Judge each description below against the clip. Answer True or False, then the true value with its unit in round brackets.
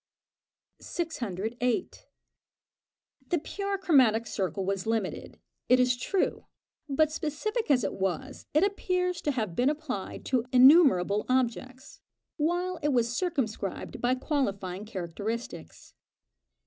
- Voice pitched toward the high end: True (255 Hz)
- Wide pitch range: True (6.4 semitones)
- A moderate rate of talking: False (110 wpm)